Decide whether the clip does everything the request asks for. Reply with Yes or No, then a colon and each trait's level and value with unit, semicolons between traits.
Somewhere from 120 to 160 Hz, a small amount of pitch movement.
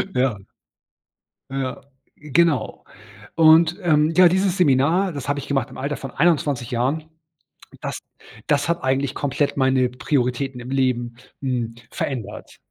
No: medium, 140 Hz; average, 3.6 semitones